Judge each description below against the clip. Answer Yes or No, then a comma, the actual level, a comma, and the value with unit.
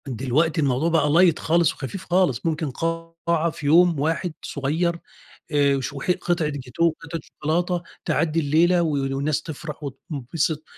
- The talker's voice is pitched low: No, medium, 160 Hz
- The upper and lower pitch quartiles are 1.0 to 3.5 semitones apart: Yes, average, 3.0 semitones